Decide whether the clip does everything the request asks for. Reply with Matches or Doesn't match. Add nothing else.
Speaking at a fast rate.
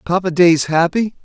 Doesn't match